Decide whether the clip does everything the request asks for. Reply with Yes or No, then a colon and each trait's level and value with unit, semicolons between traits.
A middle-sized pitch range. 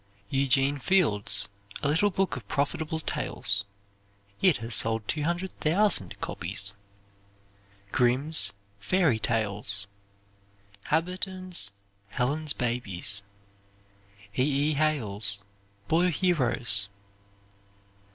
No: wide, 6.9 semitones